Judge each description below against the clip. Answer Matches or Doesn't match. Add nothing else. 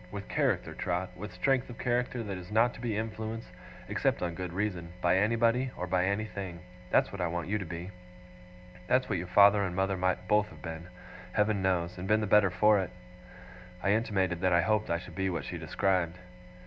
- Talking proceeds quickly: Matches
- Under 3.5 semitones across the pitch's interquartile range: Matches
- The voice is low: Matches